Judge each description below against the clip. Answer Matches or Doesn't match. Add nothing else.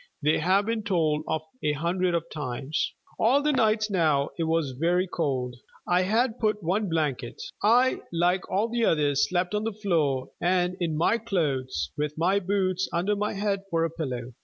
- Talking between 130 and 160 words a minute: Doesn't match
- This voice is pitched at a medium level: Matches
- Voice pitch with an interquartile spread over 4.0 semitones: Matches